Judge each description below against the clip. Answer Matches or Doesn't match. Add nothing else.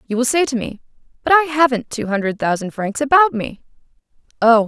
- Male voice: Doesn't match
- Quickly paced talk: Doesn't match